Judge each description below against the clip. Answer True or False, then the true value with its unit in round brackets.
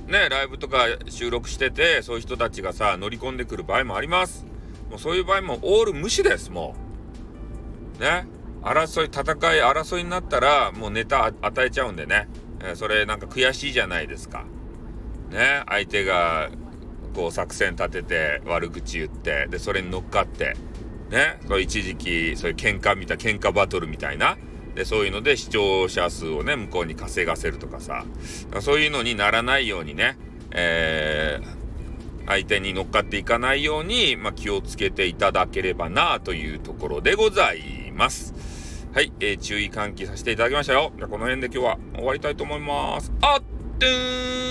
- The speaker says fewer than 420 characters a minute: True (360 characters per minute)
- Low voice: True (115 Hz)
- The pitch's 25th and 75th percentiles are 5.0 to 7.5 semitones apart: False (8.1 semitones)